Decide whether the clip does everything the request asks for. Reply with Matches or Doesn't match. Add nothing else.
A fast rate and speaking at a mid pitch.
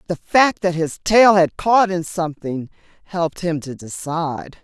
Doesn't match